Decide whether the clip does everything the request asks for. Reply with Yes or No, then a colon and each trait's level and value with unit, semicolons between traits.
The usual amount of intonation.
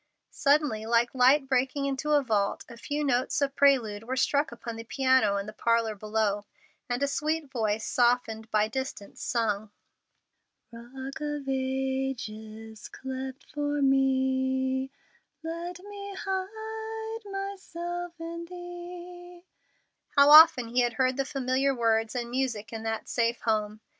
Yes: average, 4.5 semitones